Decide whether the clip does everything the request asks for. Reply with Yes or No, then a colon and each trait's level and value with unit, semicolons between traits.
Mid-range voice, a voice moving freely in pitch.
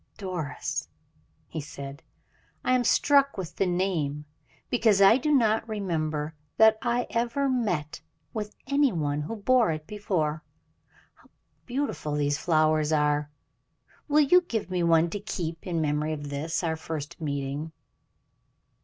Yes: medium, 170 Hz; wide, 6.7 semitones